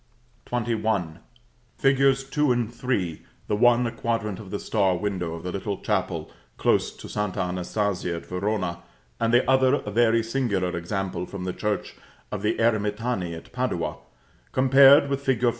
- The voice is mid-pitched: No, low, 105 Hz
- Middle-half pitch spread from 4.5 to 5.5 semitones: Yes, average, 4.9 semitones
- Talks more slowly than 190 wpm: Yes, average, 160 wpm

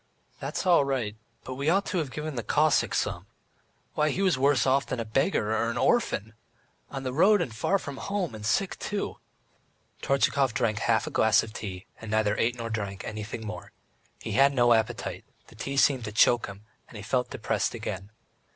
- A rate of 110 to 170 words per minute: No, average, 200 wpm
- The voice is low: Yes, low, 120 Hz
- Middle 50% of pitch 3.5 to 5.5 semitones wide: Yes, average, 4.5 semitones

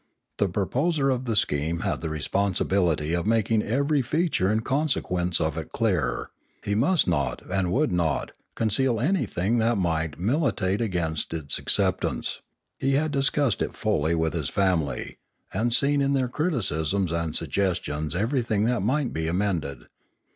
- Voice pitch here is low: Yes, low, 100 Hz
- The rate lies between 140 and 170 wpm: Yes, average, 150 wpm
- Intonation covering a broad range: Yes, wide, 7.5 semitones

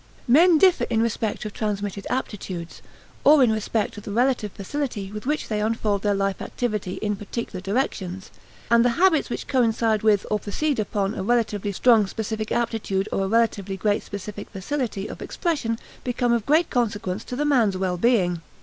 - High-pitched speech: Yes, high, 215 Hz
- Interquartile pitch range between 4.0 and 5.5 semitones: No, average, 3.4 semitones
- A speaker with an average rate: Yes, average, 175 wpm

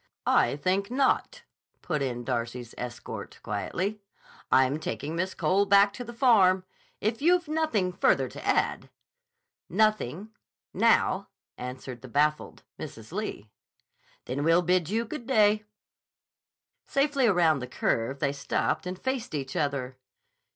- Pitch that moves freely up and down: Yes, wide, 8.3 semitones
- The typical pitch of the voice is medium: Yes, medium, 180 Hz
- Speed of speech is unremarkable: No, slow, 130 wpm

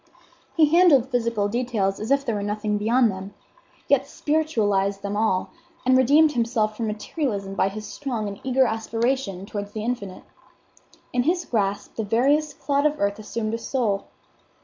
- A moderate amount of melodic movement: Yes, average, 4.6 semitones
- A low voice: No, high, 225 Hz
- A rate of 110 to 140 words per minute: No, average, 165 wpm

